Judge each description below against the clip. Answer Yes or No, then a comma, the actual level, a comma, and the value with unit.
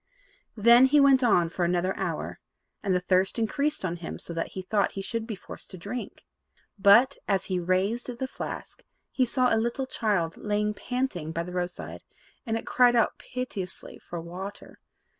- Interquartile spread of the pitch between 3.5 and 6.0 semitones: Yes, average, 5.1 semitones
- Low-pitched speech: No, high, 205 Hz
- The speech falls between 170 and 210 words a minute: Yes, average, 180 wpm